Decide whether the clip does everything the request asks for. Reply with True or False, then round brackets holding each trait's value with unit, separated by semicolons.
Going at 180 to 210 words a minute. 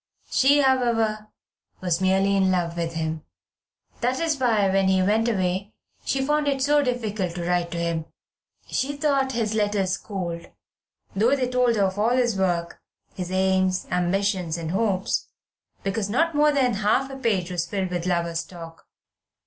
False (165 wpm)